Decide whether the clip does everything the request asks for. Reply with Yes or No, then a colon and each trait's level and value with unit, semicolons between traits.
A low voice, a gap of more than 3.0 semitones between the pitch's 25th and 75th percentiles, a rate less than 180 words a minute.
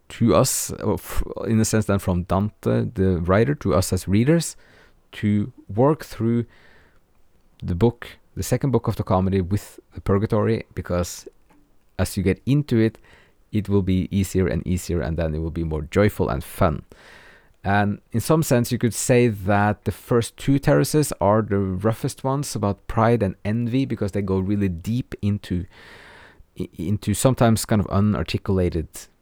Yes: low, 105 Hz; average, 3.6 semitones; average, 165 wpm